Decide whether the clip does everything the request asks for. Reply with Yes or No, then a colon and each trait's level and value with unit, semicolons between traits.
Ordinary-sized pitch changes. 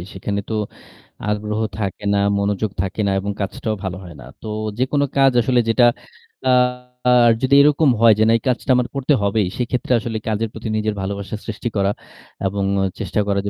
Yes: average, 3.8 semitones